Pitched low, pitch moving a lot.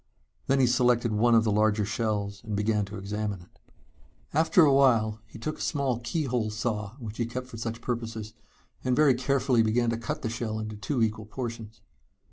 No: low, 115 Hz; narrow, 2.5 semitones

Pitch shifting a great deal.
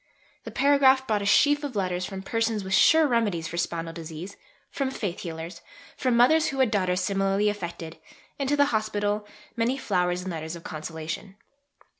Yes: wide, 6.0 semitones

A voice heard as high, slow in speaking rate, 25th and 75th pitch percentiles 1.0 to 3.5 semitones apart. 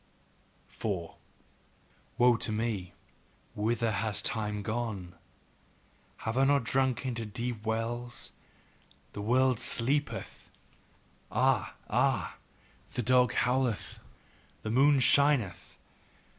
No: low, 115 Hz; slow, 95 wpm; average, 2.9 semitones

